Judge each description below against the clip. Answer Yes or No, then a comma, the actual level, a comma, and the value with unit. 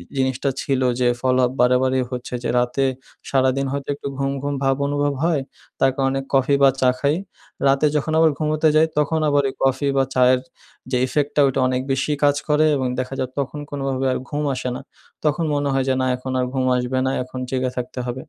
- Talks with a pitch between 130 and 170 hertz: Yes, low, 135 Hz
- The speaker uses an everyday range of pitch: No, narrow, 1.9 semitones